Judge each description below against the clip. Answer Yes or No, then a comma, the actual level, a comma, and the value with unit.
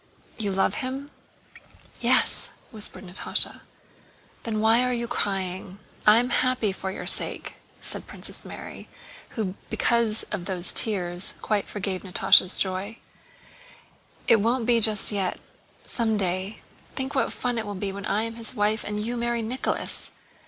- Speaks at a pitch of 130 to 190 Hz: No, high, 215 Hz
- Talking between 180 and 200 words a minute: No, average, 145 wpm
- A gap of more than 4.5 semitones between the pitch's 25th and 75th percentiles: No, average, 3.4 semitones